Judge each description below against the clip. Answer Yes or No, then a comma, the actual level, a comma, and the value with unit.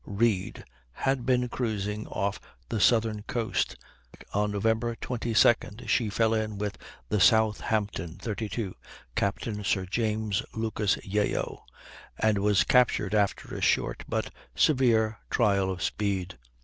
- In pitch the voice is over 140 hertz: No, low, 105 Hz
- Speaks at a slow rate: Yes, slow, 125 wpm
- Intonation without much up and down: Yes, narrow, 1.9 semitones